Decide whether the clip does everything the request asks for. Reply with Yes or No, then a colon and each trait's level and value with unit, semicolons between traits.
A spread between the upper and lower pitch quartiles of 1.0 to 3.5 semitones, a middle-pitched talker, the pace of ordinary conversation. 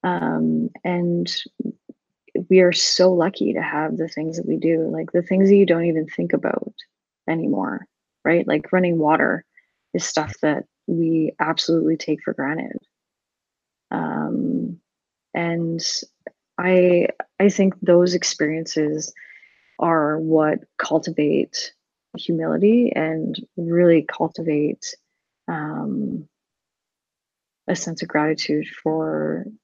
No: narrow, 2.5 semitones; medium, 165 Hz; slow, 110 wpm